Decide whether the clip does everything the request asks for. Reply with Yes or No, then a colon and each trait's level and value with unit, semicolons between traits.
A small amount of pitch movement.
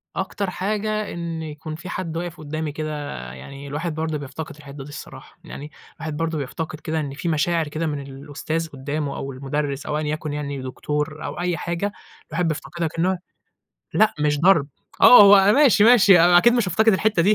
No: average, 3.3 semitones